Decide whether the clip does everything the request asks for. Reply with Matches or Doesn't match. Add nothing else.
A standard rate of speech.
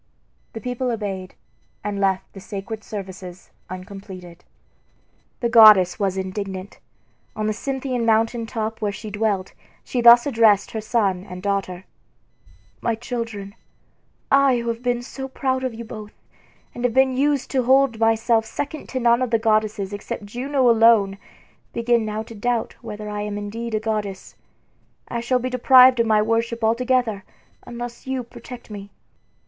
Matches